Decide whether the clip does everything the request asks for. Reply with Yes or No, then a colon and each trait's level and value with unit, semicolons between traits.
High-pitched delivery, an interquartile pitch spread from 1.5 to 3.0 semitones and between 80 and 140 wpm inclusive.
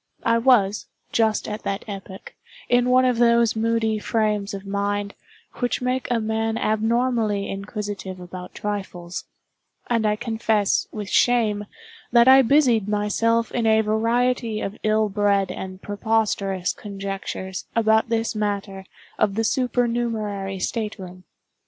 Yes: high, 215 Hz; narrow, 2.5 semitones; slow, 135 wpm